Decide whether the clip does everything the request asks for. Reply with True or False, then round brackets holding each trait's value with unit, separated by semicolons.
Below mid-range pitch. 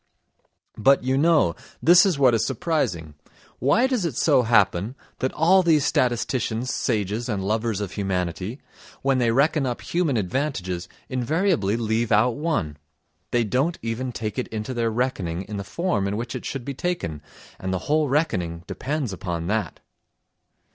True (120 Hz)